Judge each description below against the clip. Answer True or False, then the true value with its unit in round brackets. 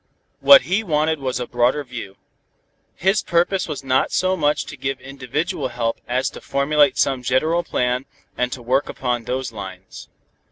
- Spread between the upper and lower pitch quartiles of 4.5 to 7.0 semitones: False (3.4 semitones)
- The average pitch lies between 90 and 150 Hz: True (135 Hz)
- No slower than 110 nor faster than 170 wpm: True (165 wpm)